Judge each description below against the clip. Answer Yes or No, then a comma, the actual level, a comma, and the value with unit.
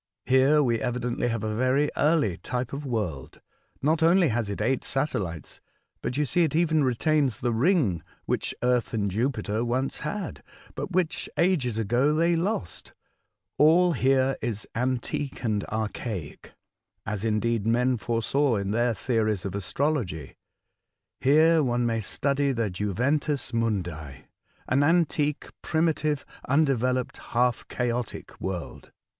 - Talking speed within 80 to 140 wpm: Yes, slow, 135 wpm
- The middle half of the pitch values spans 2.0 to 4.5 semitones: No, average, 5.0 semitones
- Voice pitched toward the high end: No, low, 125 Hz